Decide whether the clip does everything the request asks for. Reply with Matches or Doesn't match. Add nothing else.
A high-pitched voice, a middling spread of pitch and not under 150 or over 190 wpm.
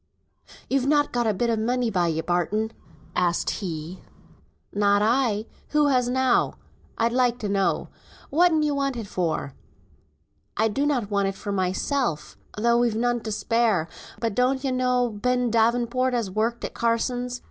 Matches